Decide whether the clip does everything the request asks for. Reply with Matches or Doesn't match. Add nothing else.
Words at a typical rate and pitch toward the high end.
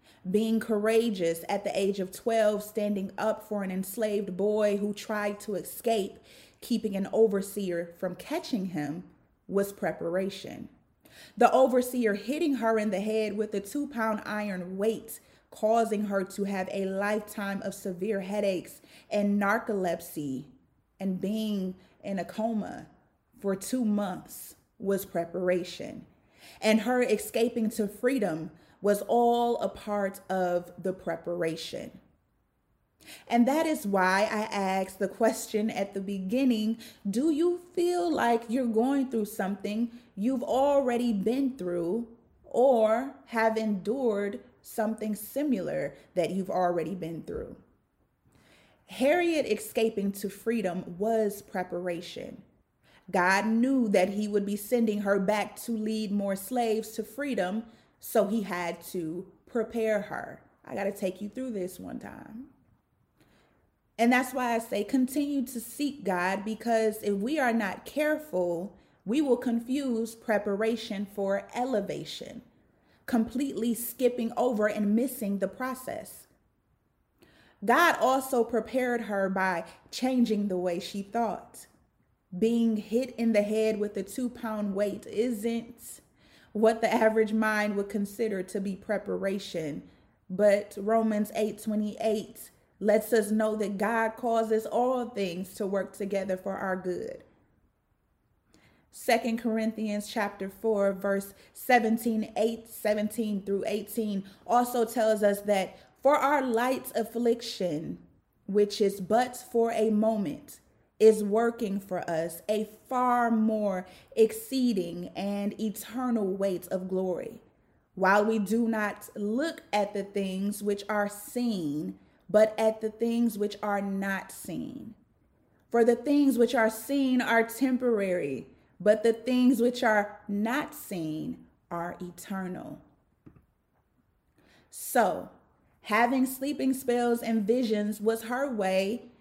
Doesn't match